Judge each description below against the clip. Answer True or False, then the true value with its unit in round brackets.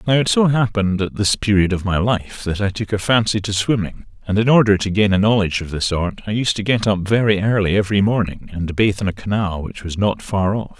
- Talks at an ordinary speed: False (255 wpm)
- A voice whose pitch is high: False (100 Hz)